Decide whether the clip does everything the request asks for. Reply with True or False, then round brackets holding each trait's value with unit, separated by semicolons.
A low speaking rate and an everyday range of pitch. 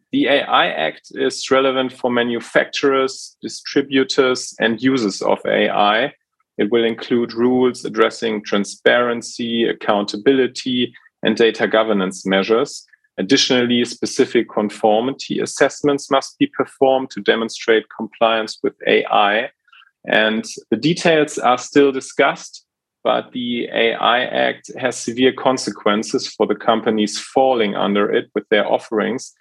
True (115 wpm; 3.2 semitones)